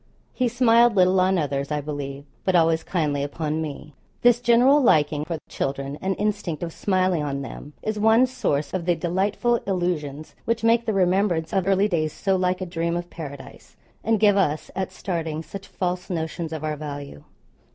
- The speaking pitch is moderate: Yes, medium, 175 Hz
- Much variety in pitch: No, average, 4.7 semitones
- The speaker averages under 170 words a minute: No, average, 185 wpm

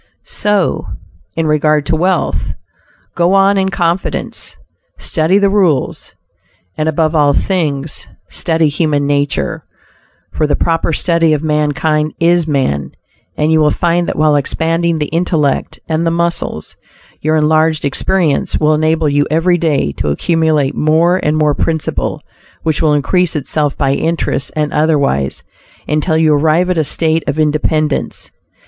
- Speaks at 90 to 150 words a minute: Yes, average, 145 wpm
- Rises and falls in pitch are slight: Yes, narrow, 2.0 semitones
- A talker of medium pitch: Yes, medium, 155 Hz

